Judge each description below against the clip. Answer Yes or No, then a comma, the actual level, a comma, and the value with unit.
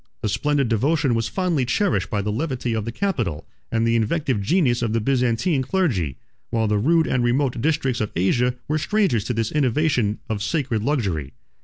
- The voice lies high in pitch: No, low, 120 Hz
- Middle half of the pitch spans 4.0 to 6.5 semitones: Yes, average, 5.3 semitones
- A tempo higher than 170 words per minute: Yes, average, 185 wpm